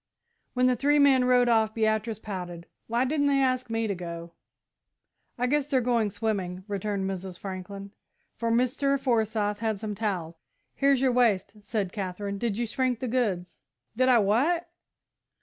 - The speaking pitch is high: Yes, high, 225 Hz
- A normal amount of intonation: Yes, average, 4.2 semitones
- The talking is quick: No, average, 165 wpm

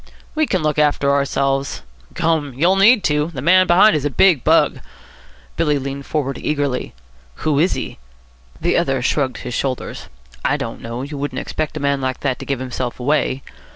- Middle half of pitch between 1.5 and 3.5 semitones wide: Yes, average, 2.9 semitones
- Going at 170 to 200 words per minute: Yes, average, 185 wpm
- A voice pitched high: No, medium, 145 Hz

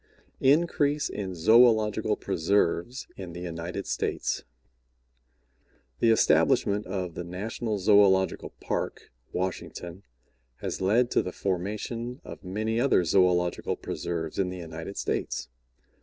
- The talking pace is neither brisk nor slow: No, slow, 110 wpm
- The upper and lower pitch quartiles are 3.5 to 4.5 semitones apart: Yes, average, 3.9 semitones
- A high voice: No, very low, 95 Hz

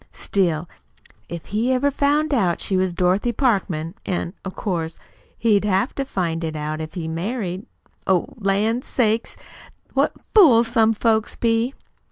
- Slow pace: No, average, 150 wpm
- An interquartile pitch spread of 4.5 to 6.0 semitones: Yes, average, 5.1 semitones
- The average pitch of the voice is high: Yes, high, 200 Hz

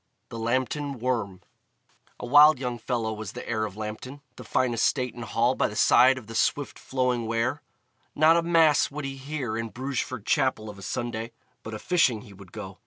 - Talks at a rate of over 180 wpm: Yes, average, 200 wpm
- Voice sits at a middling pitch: No, low, 120 Hz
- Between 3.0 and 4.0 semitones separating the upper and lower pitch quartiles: Yes, average, 3.5 semitones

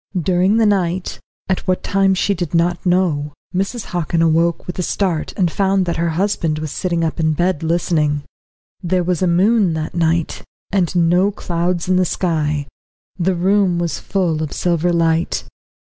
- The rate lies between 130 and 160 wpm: No, average, 175 wpm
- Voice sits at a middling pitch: Yes, medium, 175 Hz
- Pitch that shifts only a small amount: Yes, narrow, 2.2 semitones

